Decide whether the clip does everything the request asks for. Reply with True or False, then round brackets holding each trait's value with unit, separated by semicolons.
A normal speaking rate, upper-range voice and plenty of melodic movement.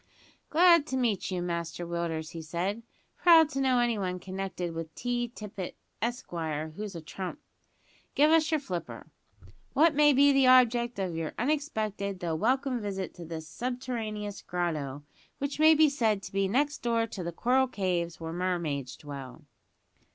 True (165 wpm; 205 Hz; 7.0 semitones)